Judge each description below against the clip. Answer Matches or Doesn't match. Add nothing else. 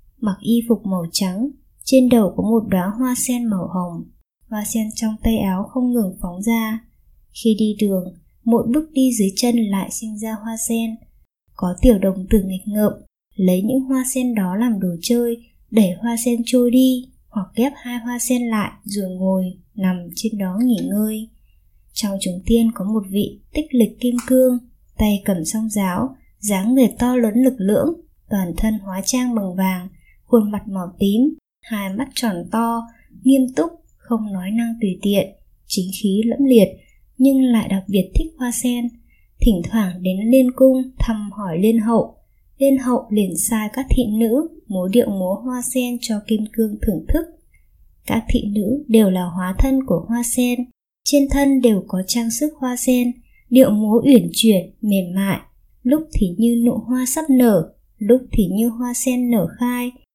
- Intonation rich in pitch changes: Doesn't match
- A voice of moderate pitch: Doesn't match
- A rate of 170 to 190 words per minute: Matches